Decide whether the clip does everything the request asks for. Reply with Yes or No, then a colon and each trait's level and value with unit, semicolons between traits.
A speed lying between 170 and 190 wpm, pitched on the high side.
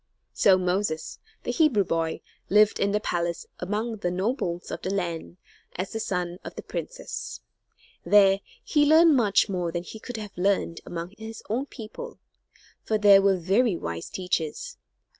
No: average, 160 wpm; high, 195 Hz